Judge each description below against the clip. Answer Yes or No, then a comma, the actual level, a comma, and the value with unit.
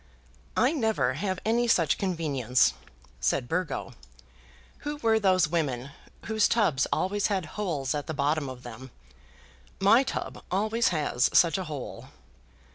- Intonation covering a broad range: Yes, wide, 7.0 semitones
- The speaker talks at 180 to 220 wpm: No, slow, 135 wpm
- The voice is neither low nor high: Yes, medium, 170 Hz